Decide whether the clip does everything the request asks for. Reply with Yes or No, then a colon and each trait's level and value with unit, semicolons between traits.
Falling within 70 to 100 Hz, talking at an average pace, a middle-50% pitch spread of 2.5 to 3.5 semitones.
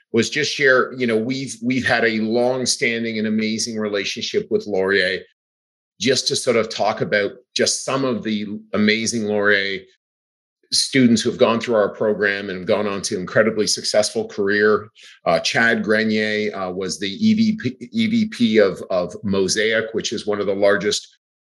No: low, 110 Hz; average, 165 wpm; average, 3.1 semitones